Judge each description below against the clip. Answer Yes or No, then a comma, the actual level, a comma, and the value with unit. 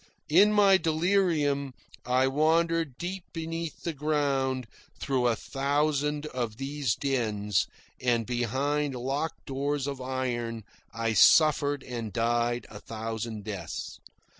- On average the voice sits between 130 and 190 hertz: Yes, low, 135 Hz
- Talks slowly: Yes, slow, 115 wpm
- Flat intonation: No, average, 4.1 semitones